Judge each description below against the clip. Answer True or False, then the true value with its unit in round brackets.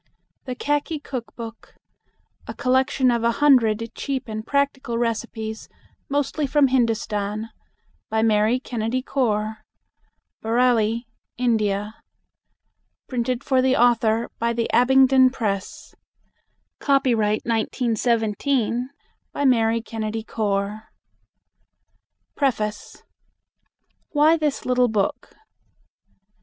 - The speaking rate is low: True (95 wpm)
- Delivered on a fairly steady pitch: False (3.0 semitones)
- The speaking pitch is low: False (235 Hz)